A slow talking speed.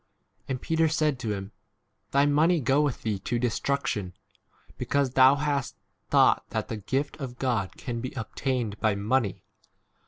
No: average, 160 wpm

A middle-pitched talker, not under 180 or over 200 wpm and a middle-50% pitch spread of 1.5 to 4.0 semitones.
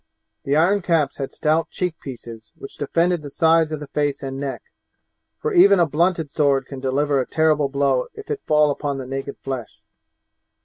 Yes: medium, 145 Hz; average, 185 wpm; average, 3.2 semitones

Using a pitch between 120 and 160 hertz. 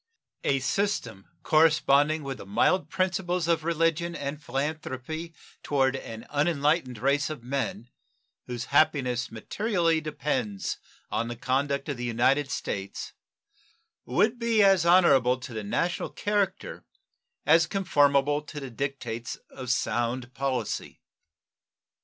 Yes: medium, 140 Hz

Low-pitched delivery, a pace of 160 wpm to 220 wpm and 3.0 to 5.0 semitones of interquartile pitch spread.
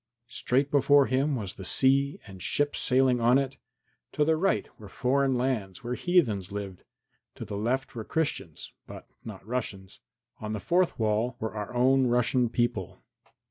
Yes: low, 125 Hz; average, 165 wpm; average, 4.3 semitones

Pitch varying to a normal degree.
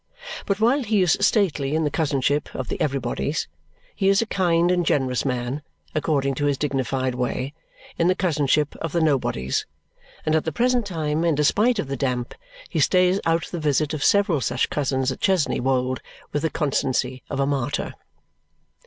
Yes: average, 4.6 semitones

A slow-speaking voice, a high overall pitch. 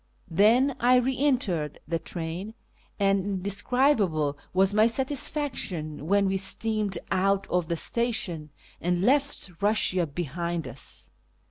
Yes: slow, 120 wpm; high, 195 Hz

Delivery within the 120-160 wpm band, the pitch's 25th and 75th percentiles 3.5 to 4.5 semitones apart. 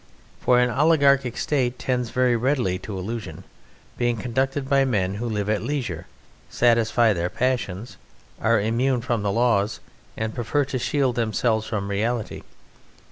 No: average, 145 wpm; average, 3.0 semitones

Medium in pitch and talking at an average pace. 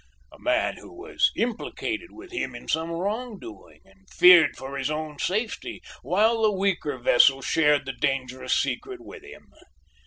Yes: medium, 175 Hz; average, 160 wpm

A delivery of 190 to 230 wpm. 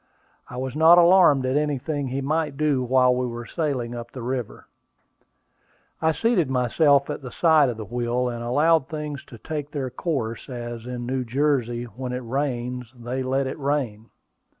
No: average, 175 wpm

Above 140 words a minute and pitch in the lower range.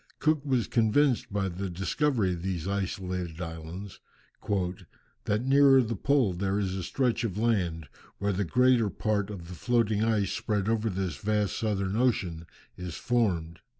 Yes: average, 155 wpm; low, 100 Hz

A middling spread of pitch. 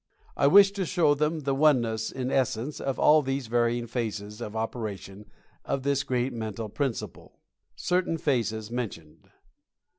Yes: average, 4.3 semitones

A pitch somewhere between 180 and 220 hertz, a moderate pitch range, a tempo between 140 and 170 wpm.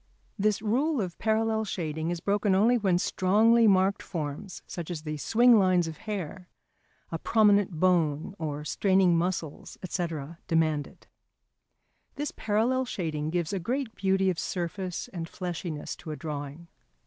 Yes: medium, 185 Hz; average, 4.3 semitones; average, 150 wpm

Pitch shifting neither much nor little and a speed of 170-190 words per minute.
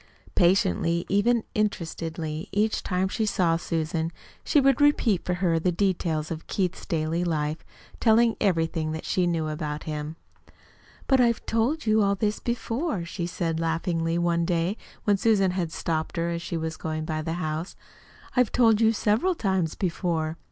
Yes: average, 4.5 semitones; average, 175 wpm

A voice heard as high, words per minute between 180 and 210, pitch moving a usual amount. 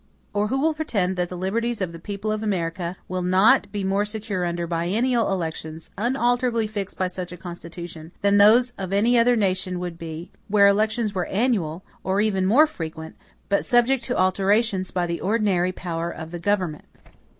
Yes: high, 195 Hz; average, 185 wpm; average, 3.8 semitones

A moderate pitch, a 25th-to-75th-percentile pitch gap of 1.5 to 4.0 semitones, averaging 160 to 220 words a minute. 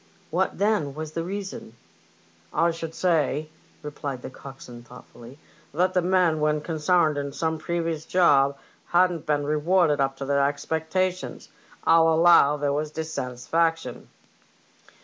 No: medium, 155 Hz; average, 3.2 semitones; average, 145 wpm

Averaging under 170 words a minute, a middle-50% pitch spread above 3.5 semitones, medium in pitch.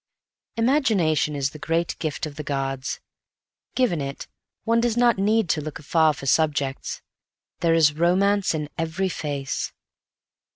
Yes: average, 140 wpm; average, 5.2 semitones; medium, 160 Hz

